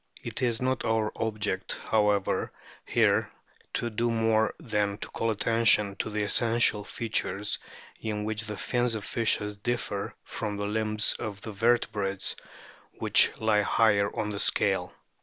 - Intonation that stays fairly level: Yes, narrow, 1.7 semitones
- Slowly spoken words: No, average, 145 wpm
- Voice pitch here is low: Yes, low, 110 Hz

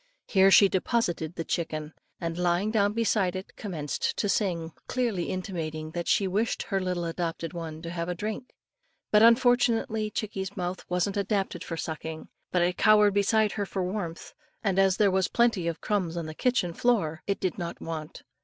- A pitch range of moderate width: Yes, average, 3.9 semitones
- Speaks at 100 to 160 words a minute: No, average, 180 wpm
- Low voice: No, medium, 185 Hz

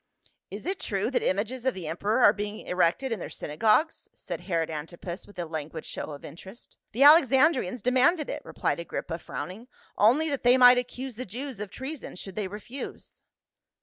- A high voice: Yes, high, 215 Hz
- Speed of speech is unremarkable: Yes, average, 180 wpm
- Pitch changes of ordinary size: No, wide, 6.3 semitones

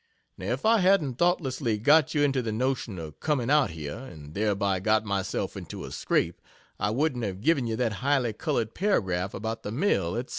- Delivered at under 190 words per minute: No, average, 195 wpm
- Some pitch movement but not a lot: No, wide, 6.0 semitones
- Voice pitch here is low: Yes, low, 115 Hz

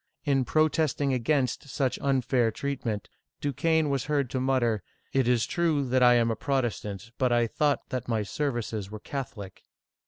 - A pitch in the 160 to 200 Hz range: No, low, 130 Hz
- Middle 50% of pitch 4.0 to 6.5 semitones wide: No, average, 3.3 semitones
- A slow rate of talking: No, average, 175 wpm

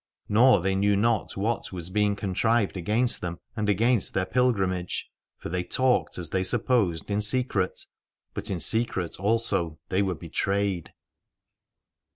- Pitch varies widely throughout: No, average, 3.7 semitones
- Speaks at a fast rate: No, average, 145 wpm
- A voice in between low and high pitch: No, low, 100 Hz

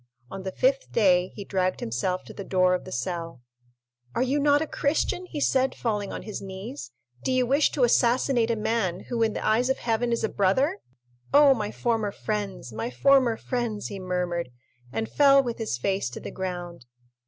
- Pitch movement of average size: No, wide, 5.7 semitones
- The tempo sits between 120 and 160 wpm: No, average, 200 wpm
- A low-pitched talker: No, high, 215 Hz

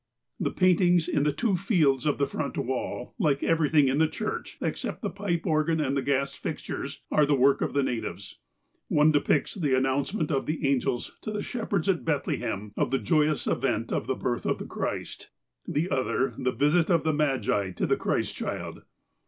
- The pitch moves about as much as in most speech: Yes, average, 3.6 semitones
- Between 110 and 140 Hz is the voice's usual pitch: No, medium, 150 Hz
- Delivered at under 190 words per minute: No, average, 195 wpm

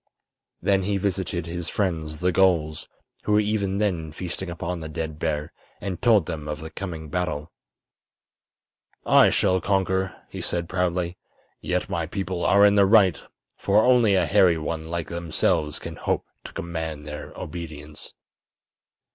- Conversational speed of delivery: Yes, average, 155 wpm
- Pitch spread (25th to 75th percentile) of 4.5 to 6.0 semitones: No, average, 3.3 semitones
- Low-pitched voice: Yes, very low, 85 Hz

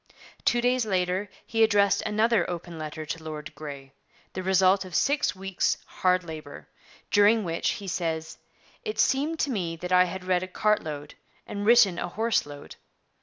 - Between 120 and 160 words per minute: No, average, 170 wpm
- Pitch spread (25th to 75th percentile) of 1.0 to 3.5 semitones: No, average, 4.3 semitones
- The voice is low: No, medium, 185 Hz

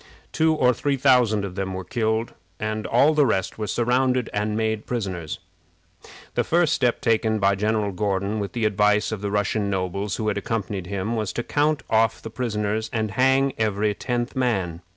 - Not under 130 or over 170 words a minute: No, average, 185 wpm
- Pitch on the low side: Yes, low, 110 Hz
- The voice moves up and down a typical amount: Yes, average, 3.2 semitones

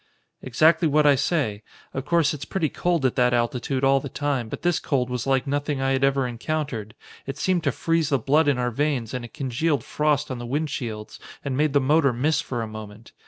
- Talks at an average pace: No, fast, 220 wpm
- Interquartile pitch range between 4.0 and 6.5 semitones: No, average, 3.4 semitones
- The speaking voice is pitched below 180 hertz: Yes, low, 135 Hz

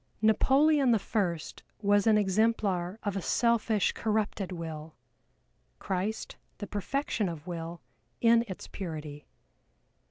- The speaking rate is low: Yes, slow, 115 wpm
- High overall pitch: Yes, high, 205 Hz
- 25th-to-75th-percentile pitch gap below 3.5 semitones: No, average, 4.2 semitones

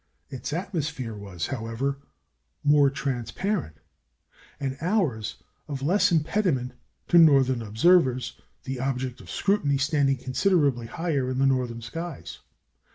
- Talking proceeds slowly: Yes, slow, 110 wpm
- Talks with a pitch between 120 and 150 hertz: Yes, low, 135 Hz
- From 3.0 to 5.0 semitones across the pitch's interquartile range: Yes, average, 4.5 semitones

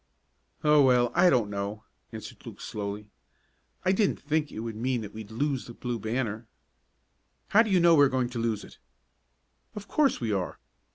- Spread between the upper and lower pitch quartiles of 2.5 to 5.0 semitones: No, wide, 5.6 semitones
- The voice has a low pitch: Yes, low, 120 Hz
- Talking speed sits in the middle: Yes, average, 185 wpm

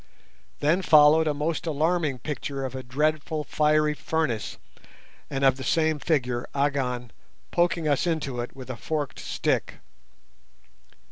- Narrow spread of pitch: No, average, 3.0 semitones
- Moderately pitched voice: Yes, medium, 150 Hz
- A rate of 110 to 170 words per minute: Yes, slow, 135 wpm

